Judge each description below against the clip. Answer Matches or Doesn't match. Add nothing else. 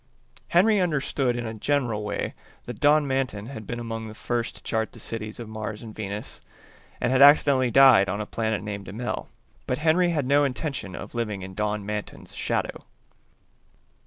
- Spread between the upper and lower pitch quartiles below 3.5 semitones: Doesn't match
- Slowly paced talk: Doesn't match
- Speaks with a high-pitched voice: Doesn't match